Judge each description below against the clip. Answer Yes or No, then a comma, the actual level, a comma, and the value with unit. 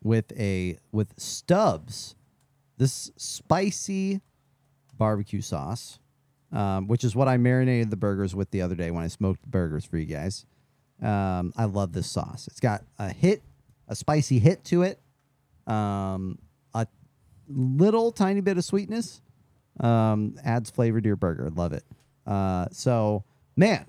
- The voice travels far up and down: Yes, wide, 5.7 semitones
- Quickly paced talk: No, average, 150 wpm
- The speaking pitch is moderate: No, low, 115 Hz